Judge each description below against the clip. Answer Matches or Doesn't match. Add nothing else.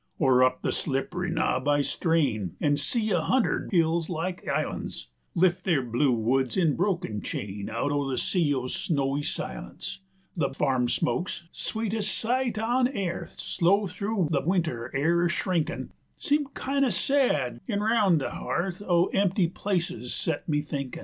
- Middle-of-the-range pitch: Matches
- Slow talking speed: Doesn't match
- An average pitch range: Doesn't match